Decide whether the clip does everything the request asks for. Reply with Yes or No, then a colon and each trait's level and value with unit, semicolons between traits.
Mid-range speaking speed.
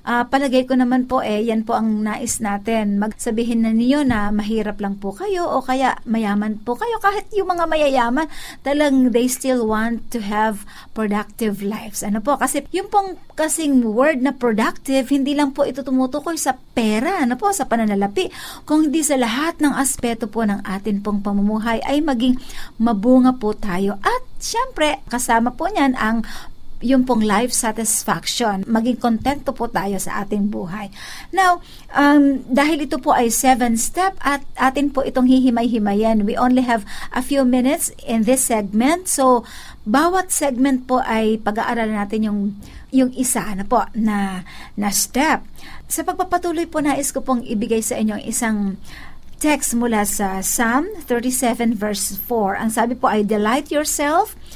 No: fast, 165 wpm